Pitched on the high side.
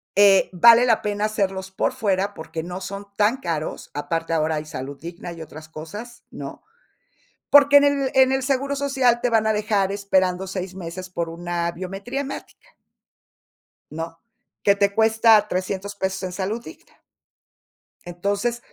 Yes: high, 195 Hz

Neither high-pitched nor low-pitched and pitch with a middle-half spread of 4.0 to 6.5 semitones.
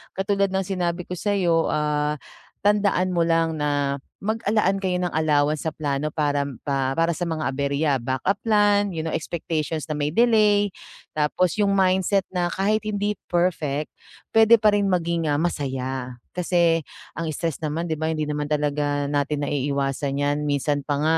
Yes: medium, 160 Hz; average, 4.6 semitones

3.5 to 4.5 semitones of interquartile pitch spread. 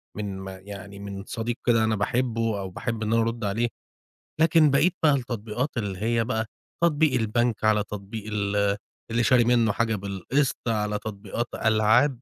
No: average, 2.8 semitones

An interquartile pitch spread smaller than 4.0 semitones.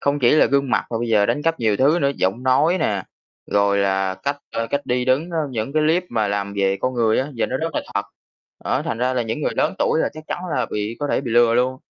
No: average, 4.6 semitones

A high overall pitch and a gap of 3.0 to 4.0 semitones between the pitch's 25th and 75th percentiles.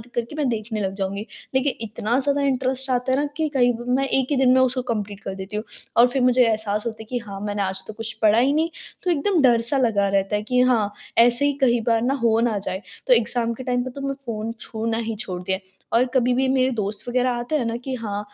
Yes: high, 235 Hz; average, 3.4 semitones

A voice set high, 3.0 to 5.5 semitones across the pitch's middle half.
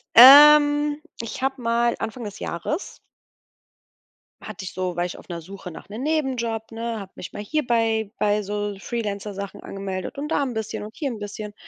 Yes: high, 220 Hz; average, 4.4 semitones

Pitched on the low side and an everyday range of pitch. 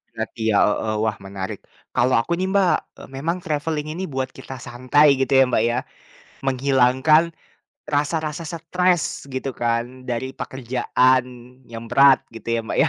Yes: low, 130 Hz; average, 4.0 semitones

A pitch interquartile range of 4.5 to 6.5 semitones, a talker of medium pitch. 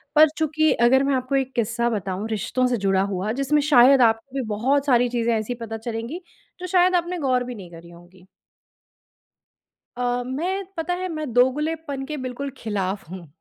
No: average, 4.8 semitones; very high, 250 Hz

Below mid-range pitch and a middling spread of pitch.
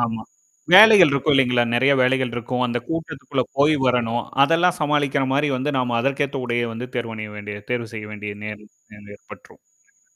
Yes: low, 125 Hz; average, 3.5 semitones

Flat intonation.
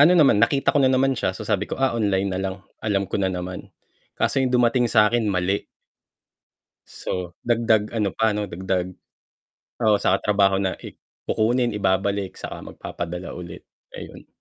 No: average, 3.7 semitones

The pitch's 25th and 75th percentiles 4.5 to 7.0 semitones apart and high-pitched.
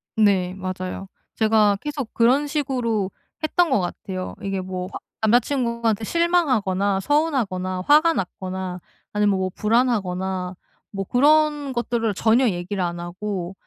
Yes: wide, 5.5 semitones; high, 210 Hz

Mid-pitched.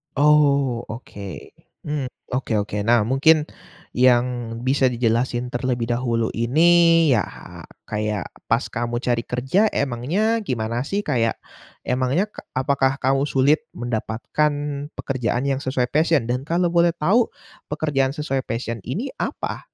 No: low, 130 Hz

